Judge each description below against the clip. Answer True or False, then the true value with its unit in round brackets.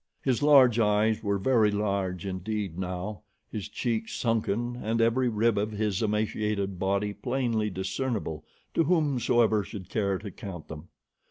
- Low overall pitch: True (105 Hz)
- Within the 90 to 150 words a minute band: True (145 wpm)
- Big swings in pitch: False (3.0 semitones)